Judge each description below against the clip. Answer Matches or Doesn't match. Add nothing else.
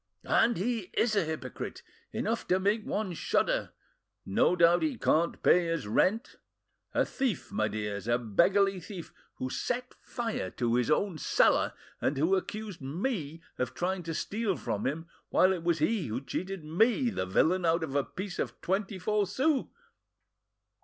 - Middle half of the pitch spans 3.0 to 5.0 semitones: Doesn't match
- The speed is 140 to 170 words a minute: Matches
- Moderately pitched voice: Matches